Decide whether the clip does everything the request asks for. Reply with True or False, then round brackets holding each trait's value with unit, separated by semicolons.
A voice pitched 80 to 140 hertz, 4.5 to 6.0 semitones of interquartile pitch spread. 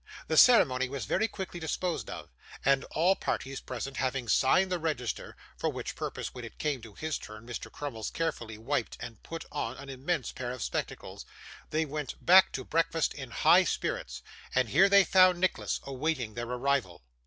True (135 Hz; 5.2 semitones)